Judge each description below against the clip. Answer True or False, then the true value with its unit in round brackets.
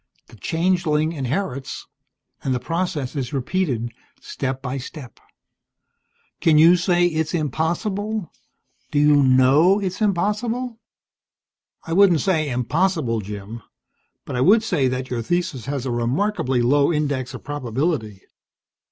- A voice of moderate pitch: True (150 Hz)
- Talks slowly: True (125 wpm)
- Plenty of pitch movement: True (5.7 semitones)